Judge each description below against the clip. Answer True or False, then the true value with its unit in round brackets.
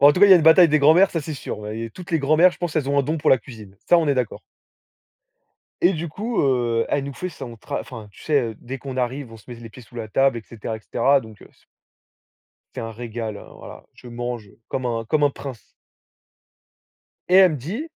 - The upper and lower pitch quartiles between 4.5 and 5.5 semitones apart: True (5.1 semitones)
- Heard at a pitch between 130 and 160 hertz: True (135 Hz)